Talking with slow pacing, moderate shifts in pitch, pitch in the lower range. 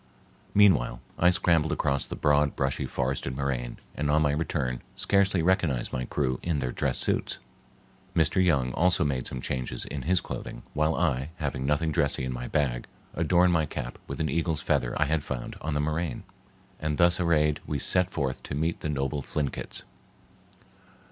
No: average, 175 wpm; average, 3.8 semitones; very low, 75 Hz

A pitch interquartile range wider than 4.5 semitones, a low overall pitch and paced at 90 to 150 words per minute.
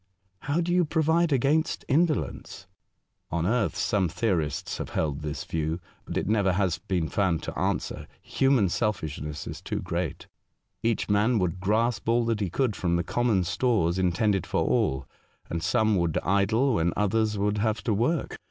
No: wide, 5.4 semitones; low, 105 Hz; average, 180 wpm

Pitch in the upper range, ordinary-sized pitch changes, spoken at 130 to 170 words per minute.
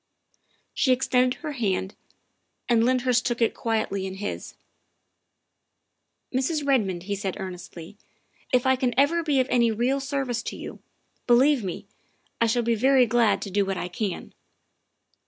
Yes: high, 240 Hz; average, 4.4 semitones; average, 160 wpm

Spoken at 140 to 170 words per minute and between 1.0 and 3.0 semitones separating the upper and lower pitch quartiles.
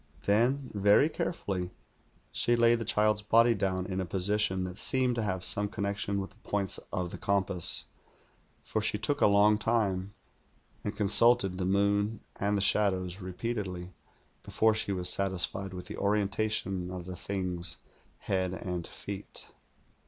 Yes: average, 155 wpm; narrow, 2.4 semitones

